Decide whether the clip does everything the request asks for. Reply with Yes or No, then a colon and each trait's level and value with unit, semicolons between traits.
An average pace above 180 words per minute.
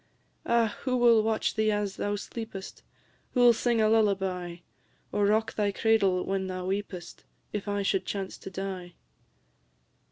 No: average, 155 wpm